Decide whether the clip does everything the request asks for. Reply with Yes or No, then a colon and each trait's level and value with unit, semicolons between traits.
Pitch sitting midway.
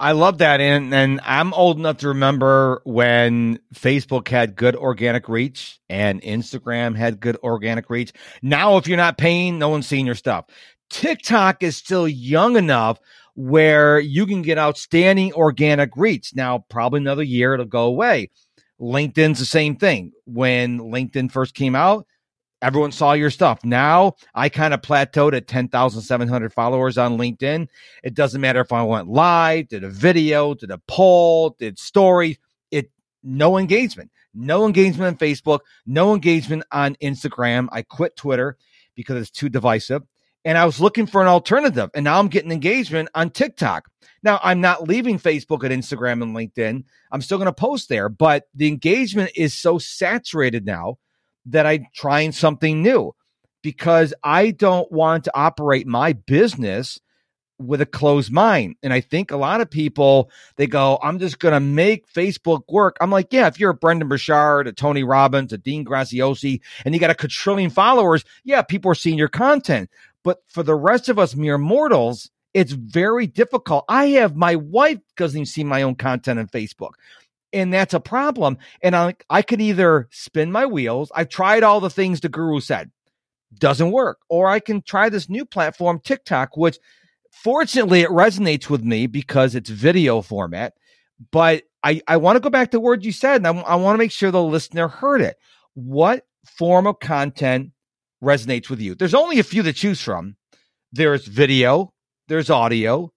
Yes: medium, 150 Hz